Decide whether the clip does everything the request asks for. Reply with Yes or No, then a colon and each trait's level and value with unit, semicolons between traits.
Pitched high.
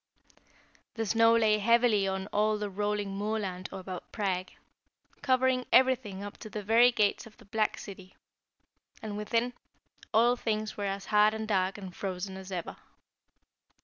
Yes: high, 210 Hz